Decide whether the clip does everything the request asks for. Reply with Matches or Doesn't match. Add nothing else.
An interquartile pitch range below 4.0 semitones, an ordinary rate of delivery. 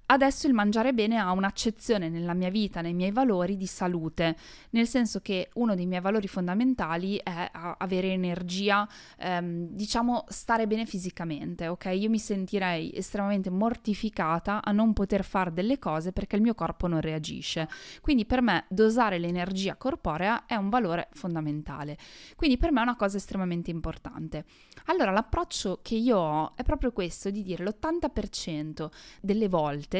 Doesn't match